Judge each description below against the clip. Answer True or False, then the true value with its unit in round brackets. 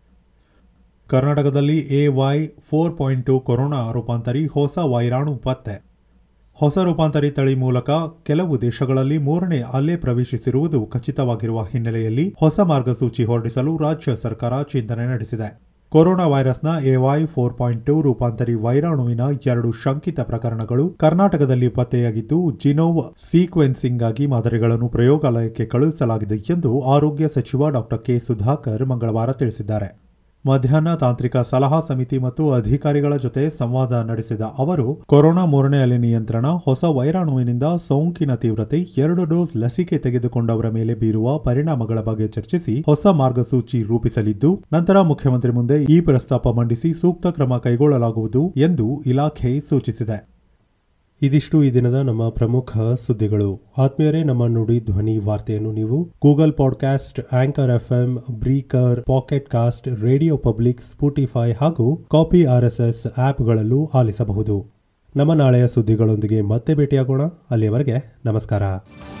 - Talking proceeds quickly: True (115 wpm)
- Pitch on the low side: True (130 Hz)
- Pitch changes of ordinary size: True (3.9 semitones)